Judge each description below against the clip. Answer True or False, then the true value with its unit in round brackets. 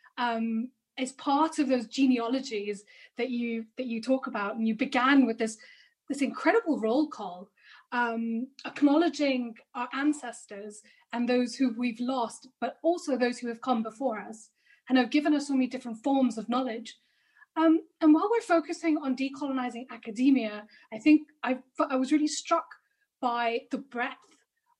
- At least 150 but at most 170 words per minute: True (160 wpm)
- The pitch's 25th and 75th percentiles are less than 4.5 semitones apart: True (3.9 semitones)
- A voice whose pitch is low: False (255 Hz)